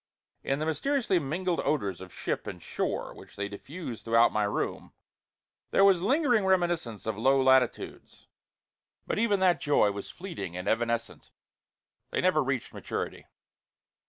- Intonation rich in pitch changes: Yes, wide, 8.4 semitones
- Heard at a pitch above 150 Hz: No, medium, 140 Hz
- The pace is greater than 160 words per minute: No, average, 145 wpm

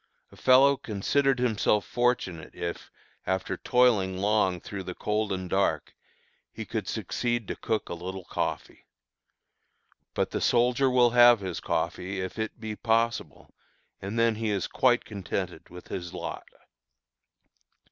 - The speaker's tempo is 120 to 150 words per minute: Yes, average, 140 wpm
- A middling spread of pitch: Yes, average, 4.3 semitones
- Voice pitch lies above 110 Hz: No, low, 105 Hz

